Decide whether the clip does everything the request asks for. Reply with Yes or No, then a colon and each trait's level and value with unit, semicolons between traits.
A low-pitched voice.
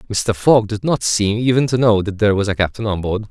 Yes: low, 110 Hz